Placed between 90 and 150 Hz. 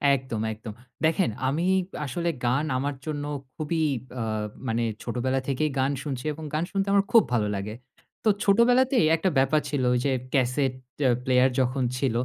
Yes: medium, 140 Hz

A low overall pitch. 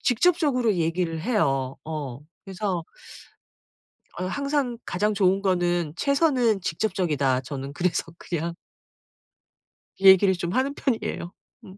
No: medium, 185 Hz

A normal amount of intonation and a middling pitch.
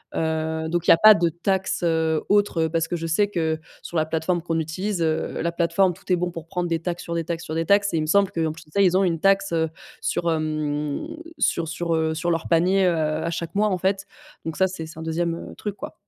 No: narrow, 2.3 semitones; medium, 165 Hz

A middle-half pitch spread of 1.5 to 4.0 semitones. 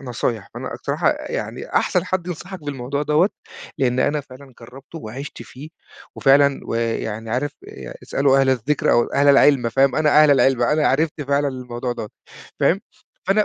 Yes: average, 3.2 semitones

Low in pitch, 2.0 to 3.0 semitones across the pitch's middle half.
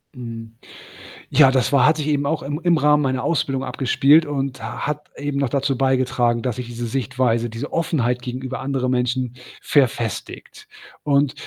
Yes: low, 130 Hz; average, 2.7 semitones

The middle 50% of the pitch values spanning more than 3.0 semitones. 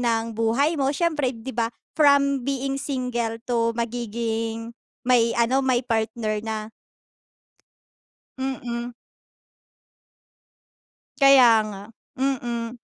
No: average, 2.7 semitones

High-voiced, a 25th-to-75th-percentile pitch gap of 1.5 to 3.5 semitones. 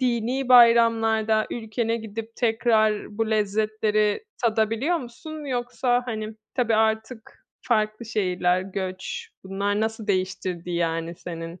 Yes: high, 220 Hz; narrow, 2.4 semitones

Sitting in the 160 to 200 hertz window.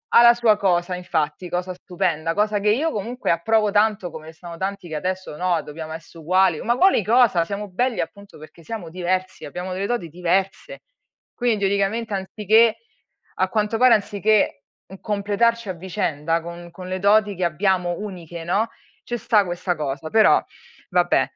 Yes: high, 190 Hz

